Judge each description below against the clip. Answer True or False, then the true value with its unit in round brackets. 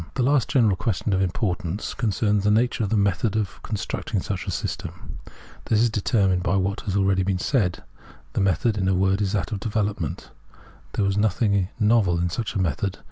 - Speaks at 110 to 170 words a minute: False (195 wpm)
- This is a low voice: True (100 Hz)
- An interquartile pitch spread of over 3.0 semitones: False (2.6 semitones)